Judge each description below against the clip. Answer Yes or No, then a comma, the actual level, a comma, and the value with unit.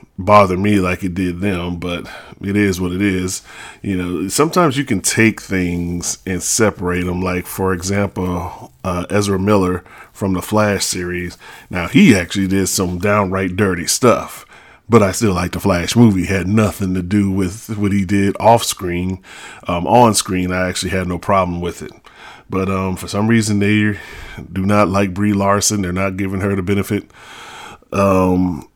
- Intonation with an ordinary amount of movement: No, narrow, 2.0 semitones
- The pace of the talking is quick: No, average, 180 wpm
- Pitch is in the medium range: No, very low, 95 Hz